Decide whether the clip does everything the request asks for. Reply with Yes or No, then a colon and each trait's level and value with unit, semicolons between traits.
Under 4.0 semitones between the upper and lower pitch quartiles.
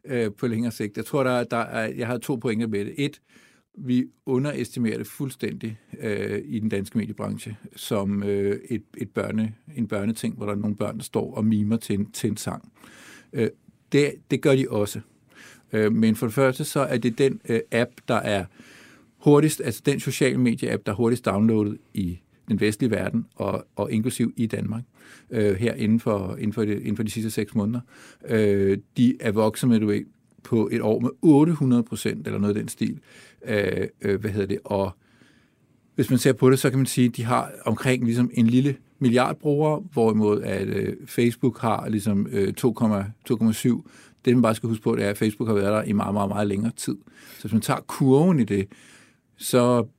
Yes: average, 3.2 semitones